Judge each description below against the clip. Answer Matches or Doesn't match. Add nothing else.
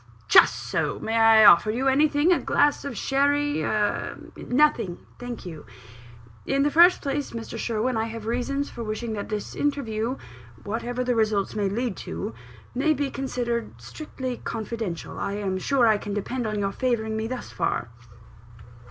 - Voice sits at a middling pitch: Doesn't match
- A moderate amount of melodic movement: Matches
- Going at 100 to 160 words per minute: Doesn't match